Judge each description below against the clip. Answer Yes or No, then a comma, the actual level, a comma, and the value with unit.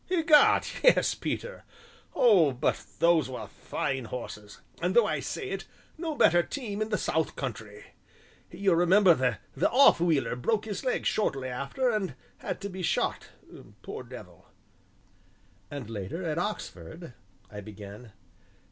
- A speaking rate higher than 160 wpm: No, average, 140 wpm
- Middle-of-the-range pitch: Yes, medium, 170 Hz